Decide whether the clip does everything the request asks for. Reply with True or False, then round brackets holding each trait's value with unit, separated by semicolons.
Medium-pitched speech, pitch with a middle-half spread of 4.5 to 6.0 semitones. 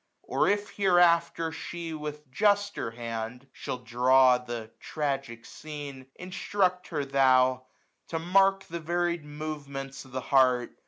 True (145 Hz; 5.0 semitones)